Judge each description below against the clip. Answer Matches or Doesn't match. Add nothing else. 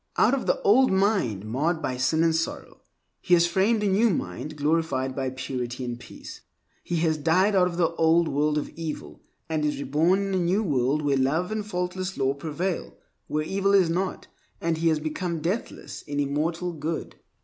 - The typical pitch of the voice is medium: Matches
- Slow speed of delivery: Doesn't match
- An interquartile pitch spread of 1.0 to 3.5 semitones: Doesn't match